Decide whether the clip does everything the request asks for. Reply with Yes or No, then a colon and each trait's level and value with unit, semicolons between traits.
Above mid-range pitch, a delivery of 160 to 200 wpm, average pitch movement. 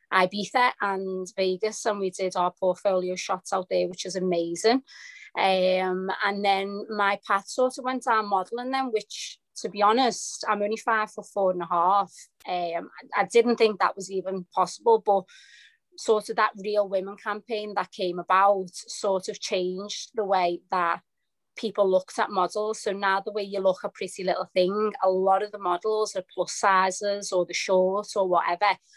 No: high, 195 Hz; average, 180 wpm; narrow, 2.2 semitones